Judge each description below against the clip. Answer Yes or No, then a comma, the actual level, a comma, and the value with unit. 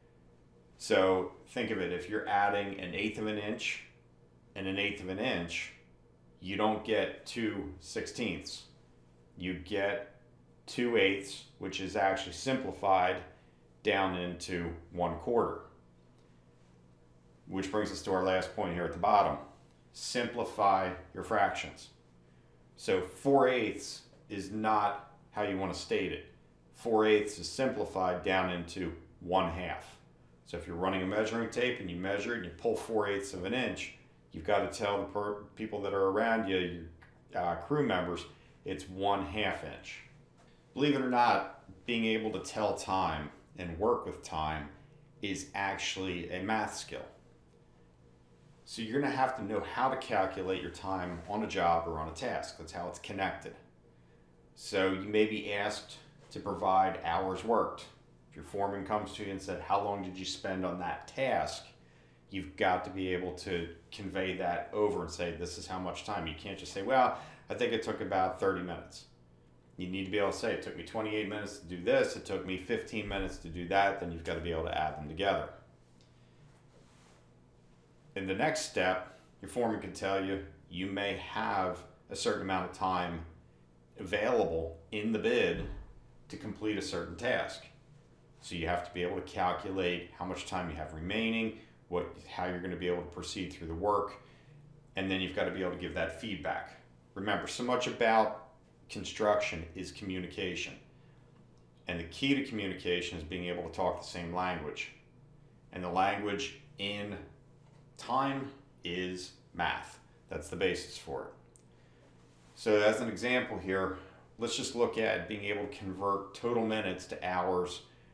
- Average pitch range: Yes, average, 3.8 semitones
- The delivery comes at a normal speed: Yes, average, 175 wpm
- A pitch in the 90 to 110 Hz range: Yes, very low, 95 Hz